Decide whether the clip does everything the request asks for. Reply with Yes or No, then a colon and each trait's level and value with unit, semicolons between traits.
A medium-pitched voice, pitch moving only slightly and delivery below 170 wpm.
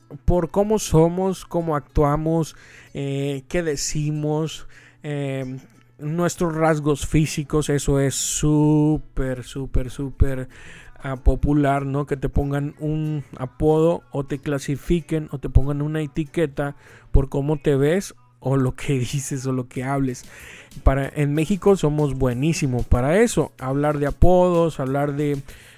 Yes: medium, 145 Hz; narrow, 2.3 semitones; average, 130 wpm